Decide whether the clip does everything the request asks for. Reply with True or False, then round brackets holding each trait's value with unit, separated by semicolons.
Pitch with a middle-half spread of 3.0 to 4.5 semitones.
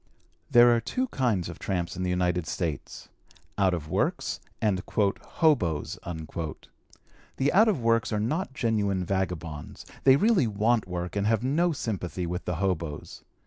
False (5.3 semitones)